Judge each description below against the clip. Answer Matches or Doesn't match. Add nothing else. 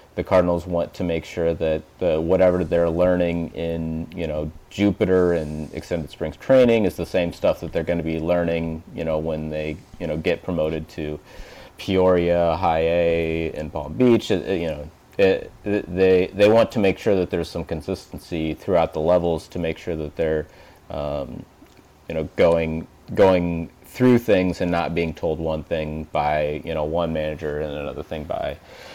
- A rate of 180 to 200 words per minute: Matches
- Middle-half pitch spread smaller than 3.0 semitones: Matches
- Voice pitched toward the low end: Matches